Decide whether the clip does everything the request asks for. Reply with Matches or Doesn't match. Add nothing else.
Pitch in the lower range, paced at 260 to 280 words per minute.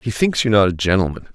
Matches